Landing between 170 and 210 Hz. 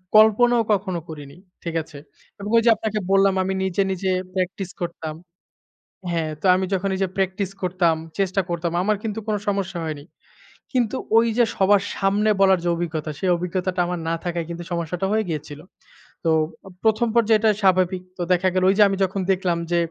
Yes: high, 190 Hz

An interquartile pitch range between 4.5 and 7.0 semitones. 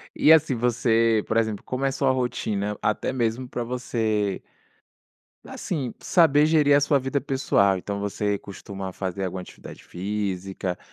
Yes: average, 4.8 semitones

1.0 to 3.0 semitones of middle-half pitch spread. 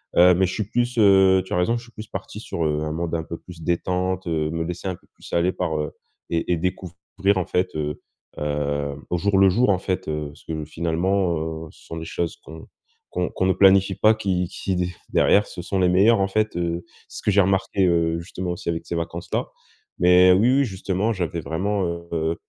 Yes: average, 2.7 semitones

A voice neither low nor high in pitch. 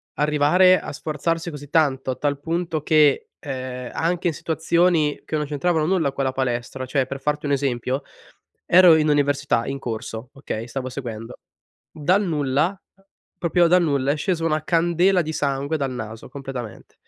Yes: medium, 145 Hz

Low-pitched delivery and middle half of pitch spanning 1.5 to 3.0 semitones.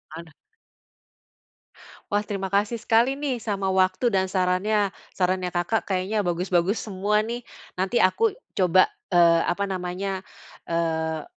No: high, 190 Hz; average, 2.7 semitones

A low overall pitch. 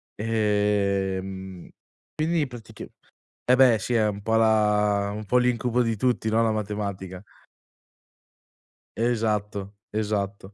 Yes: low, 105 Hz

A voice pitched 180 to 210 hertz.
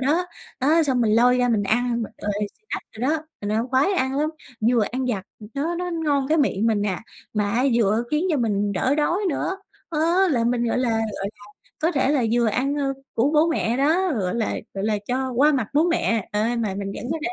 No: very high, 250 Hz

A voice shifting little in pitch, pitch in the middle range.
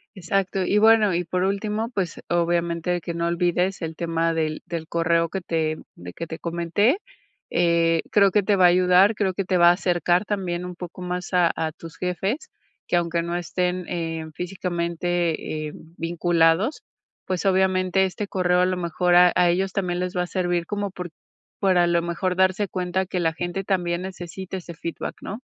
Yes: narrow, 1.8 semitones; medium, 180 Hz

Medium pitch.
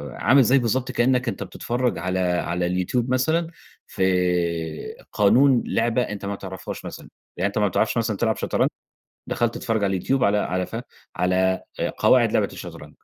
No: low, 105 Hz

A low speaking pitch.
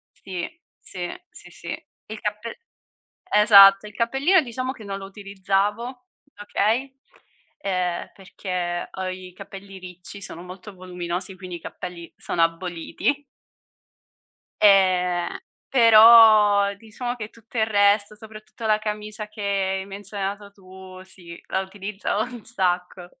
No: high, 200 Hz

